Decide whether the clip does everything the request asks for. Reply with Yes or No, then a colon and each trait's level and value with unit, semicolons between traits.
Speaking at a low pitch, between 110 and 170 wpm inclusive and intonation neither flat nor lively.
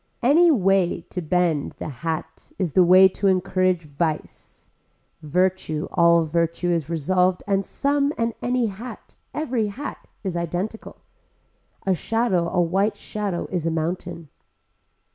No: medium, 180 Hz; slow, 135 wpm; average, 3.4 semitones